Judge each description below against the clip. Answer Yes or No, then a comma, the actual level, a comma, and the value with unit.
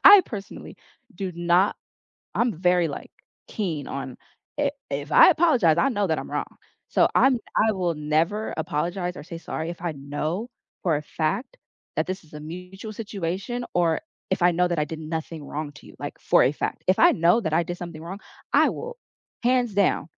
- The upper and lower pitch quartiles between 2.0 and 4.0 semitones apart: No, average, 4.4 semitones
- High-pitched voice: No, medium, 175 Hz